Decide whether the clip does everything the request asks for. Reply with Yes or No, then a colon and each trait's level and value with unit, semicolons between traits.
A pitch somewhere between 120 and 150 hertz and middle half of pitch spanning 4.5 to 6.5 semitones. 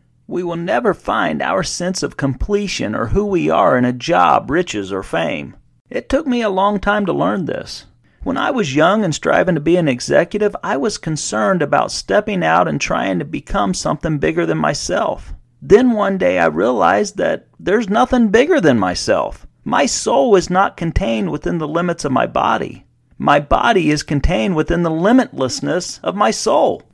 No: medium, 180 Hz; average, 4.9 semitones